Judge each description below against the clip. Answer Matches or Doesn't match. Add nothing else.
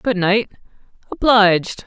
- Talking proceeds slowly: Matches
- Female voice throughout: Matches